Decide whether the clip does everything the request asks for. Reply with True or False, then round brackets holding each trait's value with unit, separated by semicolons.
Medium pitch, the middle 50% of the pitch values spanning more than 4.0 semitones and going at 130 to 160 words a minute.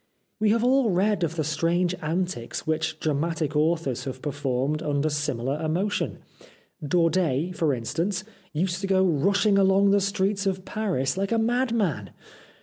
True (170 Hz; 4.8 semitones; 145 wpm)